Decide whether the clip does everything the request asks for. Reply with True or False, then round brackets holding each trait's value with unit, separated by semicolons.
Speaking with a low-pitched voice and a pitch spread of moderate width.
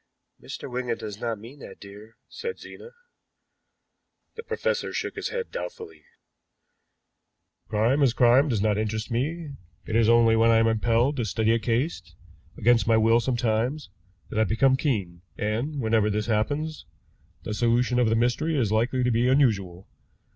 True (115 Hz; 3.6 semitones)